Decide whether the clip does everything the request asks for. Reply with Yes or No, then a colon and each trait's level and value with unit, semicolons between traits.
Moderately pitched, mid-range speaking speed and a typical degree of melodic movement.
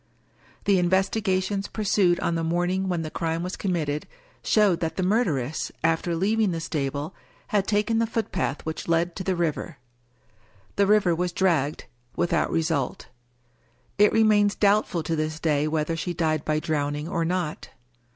Yes: medium, 175 Hz; average, 160 wpm; average, 3.6 semitones